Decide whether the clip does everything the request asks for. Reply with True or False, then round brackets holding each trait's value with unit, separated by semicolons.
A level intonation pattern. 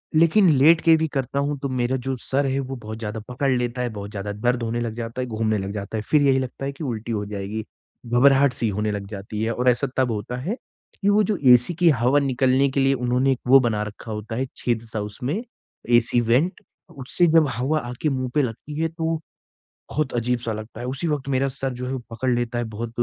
False (3.4 semitones)